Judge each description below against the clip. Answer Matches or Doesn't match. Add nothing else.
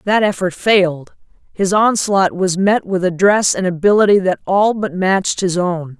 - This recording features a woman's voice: Matches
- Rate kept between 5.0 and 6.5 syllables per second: Doesn't match